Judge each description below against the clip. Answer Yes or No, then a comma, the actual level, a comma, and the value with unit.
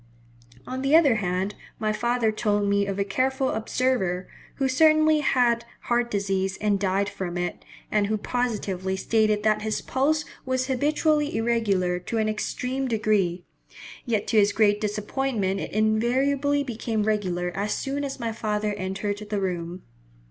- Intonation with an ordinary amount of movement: Yes, average, 4.3 semitones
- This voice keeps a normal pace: Yes, average, 155 wpm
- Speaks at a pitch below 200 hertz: No, high, 215 Hz